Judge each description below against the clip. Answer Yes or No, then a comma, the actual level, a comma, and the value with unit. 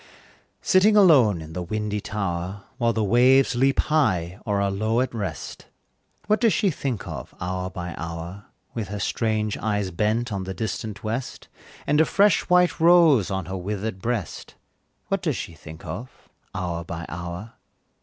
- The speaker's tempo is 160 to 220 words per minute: Yes, average, 165 wpm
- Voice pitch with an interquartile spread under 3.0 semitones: No, average, 5.3 semitones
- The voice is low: Yes, low, 105 Hz